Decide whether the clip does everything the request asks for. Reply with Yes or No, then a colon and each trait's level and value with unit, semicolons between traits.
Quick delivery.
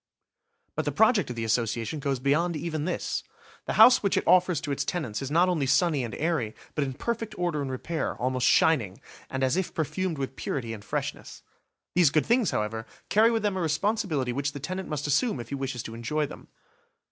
Yes: fast, 210 wpm